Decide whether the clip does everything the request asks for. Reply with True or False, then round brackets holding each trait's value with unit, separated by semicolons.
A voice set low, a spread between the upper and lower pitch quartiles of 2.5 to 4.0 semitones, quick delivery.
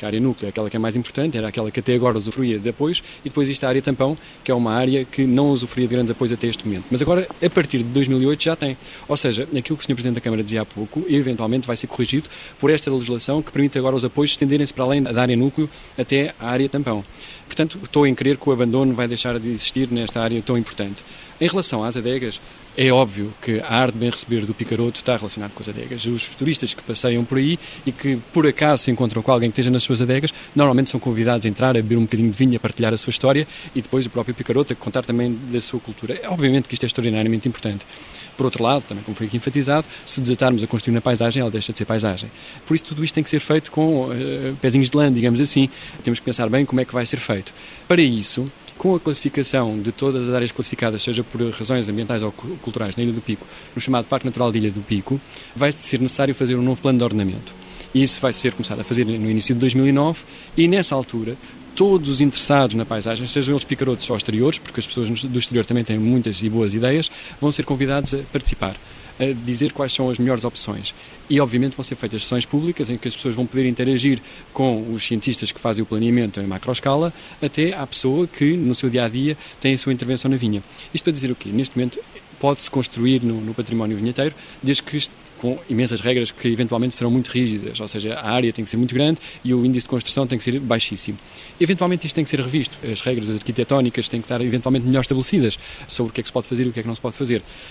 True (125 Hz; 2.9 semitones; 245 wpm)